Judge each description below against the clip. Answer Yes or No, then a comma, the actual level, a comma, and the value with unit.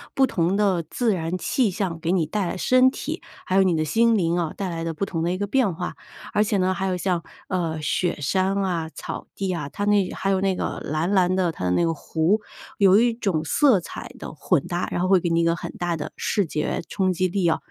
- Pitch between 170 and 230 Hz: Yes, medium, 185 Hz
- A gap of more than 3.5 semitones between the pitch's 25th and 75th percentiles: No, average, 2.9 semitones